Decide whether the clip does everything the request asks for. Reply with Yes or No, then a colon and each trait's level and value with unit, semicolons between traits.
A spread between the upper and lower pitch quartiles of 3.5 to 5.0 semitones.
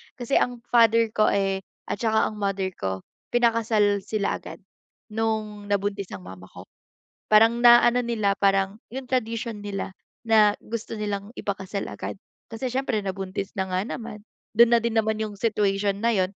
No: average, 2.7 semitones